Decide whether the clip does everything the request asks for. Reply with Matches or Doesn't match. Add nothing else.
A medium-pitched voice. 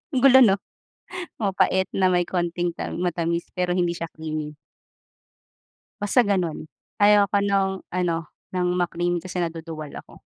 Matches